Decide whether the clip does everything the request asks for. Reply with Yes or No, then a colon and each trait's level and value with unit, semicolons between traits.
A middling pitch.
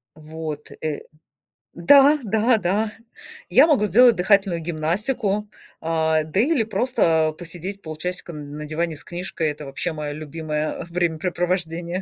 Yes: medium, 170 Hz